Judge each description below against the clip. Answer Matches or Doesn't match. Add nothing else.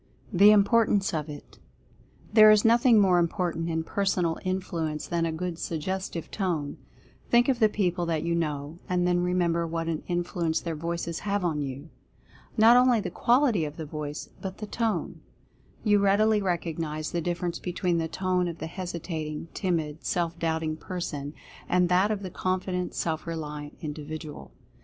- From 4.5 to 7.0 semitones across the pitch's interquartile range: Doesn't match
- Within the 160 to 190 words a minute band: Matches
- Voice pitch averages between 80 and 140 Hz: Doesn't match